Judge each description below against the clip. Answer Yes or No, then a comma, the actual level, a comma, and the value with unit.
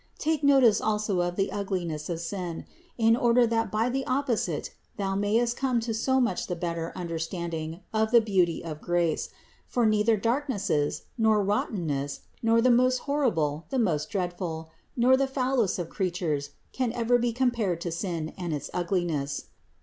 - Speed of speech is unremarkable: Yes, average, 170 wpm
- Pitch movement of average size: No, wide, 5.8 semitones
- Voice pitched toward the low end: No, high, 200 Hz